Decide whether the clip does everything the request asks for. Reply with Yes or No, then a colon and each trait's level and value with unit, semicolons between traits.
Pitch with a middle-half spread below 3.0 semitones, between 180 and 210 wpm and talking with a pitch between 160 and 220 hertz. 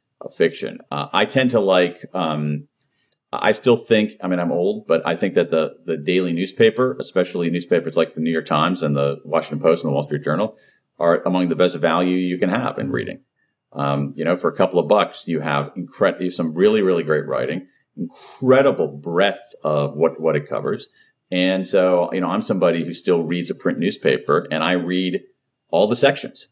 No: narrow, 2.4 semitones; fast, 205 wpm; very low, 90 Hz